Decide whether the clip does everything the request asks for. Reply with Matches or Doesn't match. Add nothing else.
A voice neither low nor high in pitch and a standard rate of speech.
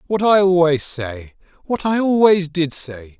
Matches